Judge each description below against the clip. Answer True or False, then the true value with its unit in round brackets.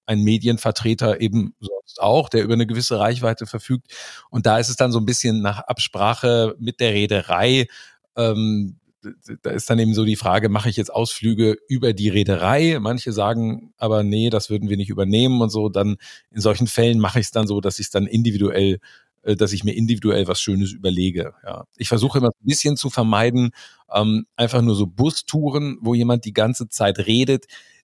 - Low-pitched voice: True (115 Hz)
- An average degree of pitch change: False (2.2 semitones)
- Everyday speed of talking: False (195 wpm)